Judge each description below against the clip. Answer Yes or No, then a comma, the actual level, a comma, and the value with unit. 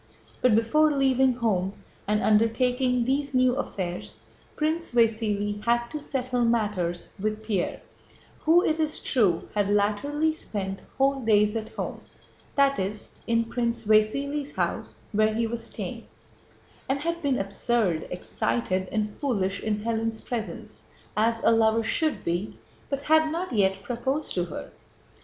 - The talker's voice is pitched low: No, high, 230 Hz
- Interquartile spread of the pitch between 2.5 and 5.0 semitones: Yes, average, 4.4 semitones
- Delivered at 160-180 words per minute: No, average, 145 wpm